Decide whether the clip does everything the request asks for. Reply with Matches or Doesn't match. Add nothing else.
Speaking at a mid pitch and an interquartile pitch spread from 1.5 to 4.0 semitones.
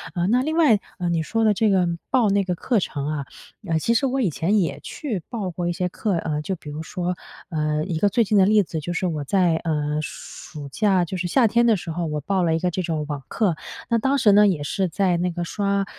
Doesn't match